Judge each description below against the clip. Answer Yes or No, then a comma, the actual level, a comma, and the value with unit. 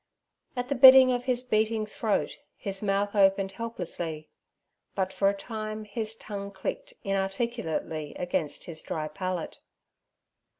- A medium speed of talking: No, slow, 130 wpm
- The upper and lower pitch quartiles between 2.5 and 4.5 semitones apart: Yes, average, 3.3 semitones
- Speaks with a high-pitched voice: Yes, high, 200 Hz